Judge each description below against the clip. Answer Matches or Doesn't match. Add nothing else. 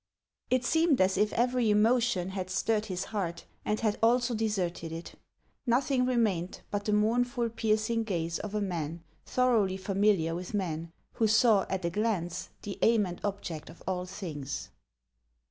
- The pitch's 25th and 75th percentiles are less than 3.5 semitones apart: Doesn't match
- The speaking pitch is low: Doesn't match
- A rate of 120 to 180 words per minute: Matches